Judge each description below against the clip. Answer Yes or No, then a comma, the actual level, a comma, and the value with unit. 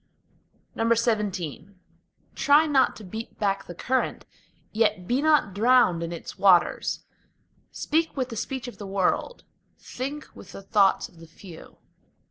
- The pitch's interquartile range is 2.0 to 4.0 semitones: No, wide, 5.5 semitones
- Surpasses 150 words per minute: No, average, 140 wpm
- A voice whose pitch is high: Yes, high, 215 Hz